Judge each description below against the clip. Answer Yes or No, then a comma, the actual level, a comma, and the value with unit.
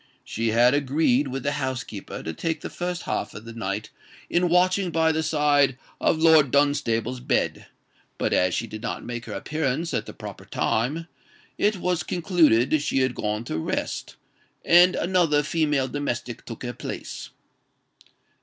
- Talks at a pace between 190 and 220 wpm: No, average, 165 wpm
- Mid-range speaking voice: Yes, medium, 145 Hz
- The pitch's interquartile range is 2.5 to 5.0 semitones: No, wide, 5.4 semitones